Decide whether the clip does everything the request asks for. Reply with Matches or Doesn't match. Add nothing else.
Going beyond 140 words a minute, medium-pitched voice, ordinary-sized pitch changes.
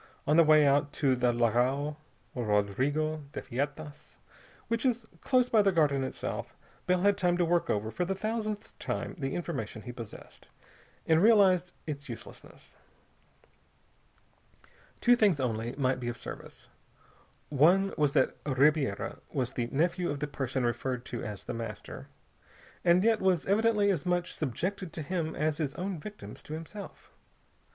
Doesn't match